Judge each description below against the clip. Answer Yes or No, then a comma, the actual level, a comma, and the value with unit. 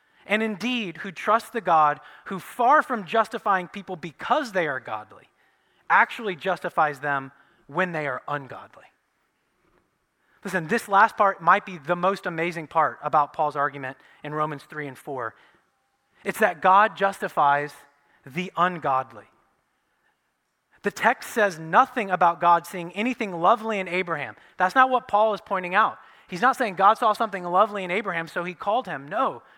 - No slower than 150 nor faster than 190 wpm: Yes, average, 160 wpm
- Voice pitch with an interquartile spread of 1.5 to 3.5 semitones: No, average, 5.2 semitones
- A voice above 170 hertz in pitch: Yes, medium, 185 Hz